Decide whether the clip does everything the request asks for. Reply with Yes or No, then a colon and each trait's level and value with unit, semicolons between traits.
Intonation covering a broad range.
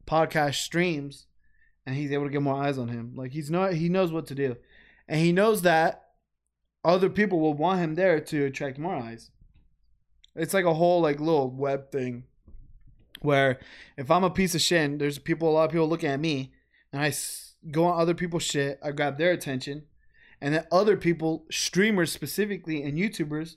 No: average, 3.7 semitones